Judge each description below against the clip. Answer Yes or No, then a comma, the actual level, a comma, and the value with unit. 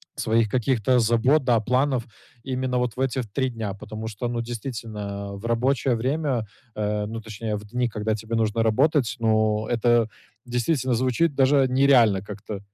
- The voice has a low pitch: Yes, low, 115 Hz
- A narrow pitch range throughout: No, average, 3.0 semitones